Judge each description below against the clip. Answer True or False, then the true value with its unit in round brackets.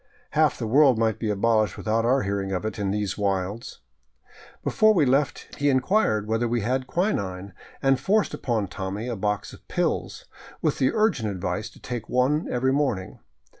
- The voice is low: True (115 Hz)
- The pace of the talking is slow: False (175 wpm)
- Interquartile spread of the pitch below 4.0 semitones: False (4.7 semitones)